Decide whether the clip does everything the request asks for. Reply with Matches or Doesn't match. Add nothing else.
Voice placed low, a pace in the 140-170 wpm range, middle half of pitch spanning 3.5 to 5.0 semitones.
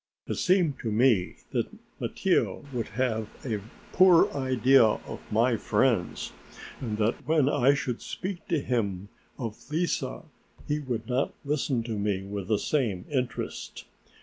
Matches